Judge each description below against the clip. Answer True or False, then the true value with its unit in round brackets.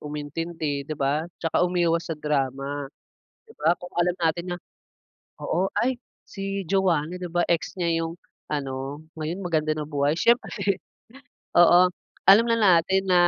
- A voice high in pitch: False (170 Hz)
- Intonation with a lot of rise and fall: False (3.4 semitones)